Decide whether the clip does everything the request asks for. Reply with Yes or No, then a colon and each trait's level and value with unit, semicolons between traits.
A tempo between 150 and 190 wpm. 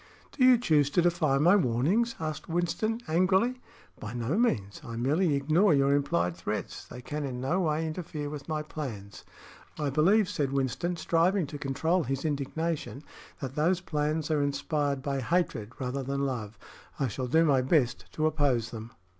Yes: average, 170 wpm